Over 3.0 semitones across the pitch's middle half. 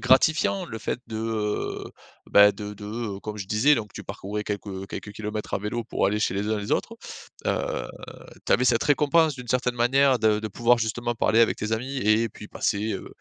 No: average, 2.7 semitones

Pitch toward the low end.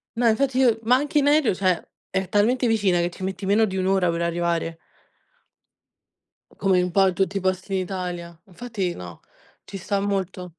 No: high, 190 Hz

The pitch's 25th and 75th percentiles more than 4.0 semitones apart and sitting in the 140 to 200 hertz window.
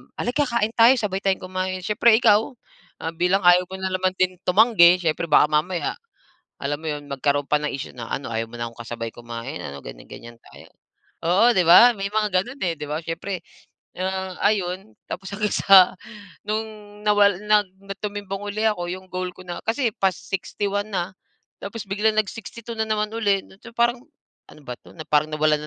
Yes: average, 4.9 semitones; medium, 185 Hz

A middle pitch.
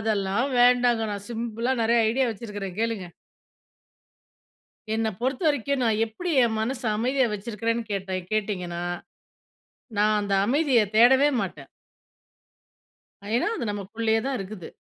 No: high, 225 Hz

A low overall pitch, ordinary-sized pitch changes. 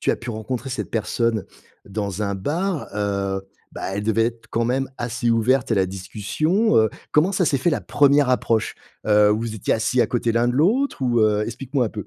Yes: low, 115 Hz; average, 4.1 semitones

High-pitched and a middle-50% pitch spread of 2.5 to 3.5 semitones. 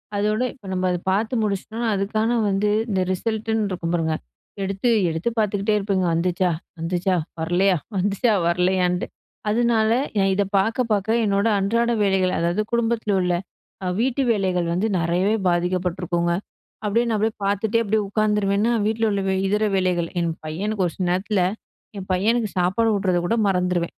Yes: high, 195 Hz; average, 3.2 semitones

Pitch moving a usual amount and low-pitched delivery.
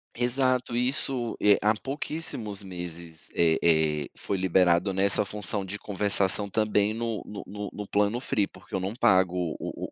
Yes: average, 3.2 semitones; low, 100 Hz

